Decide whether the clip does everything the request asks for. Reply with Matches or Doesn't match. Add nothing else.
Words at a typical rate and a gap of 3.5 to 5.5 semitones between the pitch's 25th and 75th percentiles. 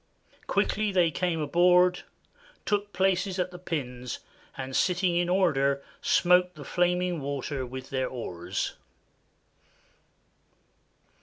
Doesn't match